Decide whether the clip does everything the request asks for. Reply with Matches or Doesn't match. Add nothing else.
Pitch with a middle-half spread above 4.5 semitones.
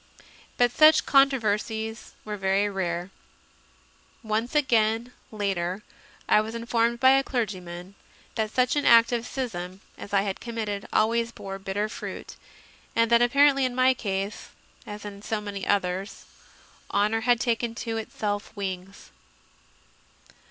Doesn't match